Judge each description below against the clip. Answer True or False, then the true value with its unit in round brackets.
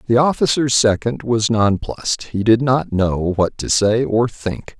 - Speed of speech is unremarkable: True (175 wpm)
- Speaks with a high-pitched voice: False (115 Hz)